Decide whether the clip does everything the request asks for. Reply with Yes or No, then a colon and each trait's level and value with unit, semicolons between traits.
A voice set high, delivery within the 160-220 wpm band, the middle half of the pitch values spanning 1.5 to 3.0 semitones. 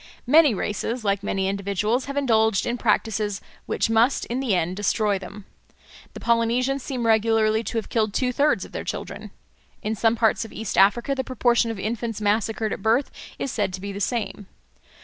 Yes: high, 225 Hz; average, 190 wpm; average, 2.7 semitones